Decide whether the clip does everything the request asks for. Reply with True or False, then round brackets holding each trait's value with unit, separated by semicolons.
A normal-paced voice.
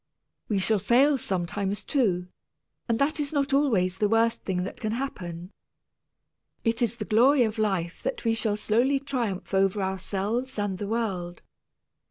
True (160 wpm)